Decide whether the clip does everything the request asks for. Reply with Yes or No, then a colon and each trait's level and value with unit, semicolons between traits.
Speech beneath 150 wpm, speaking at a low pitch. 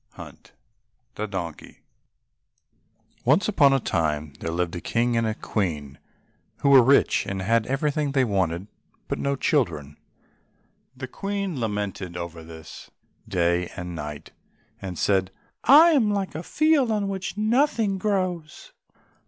Yes: slow, 135 wpm; low, 115 Hz